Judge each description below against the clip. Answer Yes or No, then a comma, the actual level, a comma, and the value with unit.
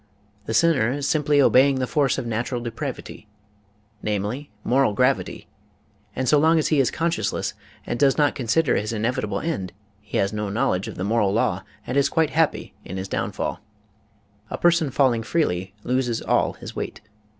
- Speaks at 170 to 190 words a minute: Yes, average, 175 wpm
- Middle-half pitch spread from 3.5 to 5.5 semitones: Yes, average, 5.2 semitones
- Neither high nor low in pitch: No, low, 125 Hz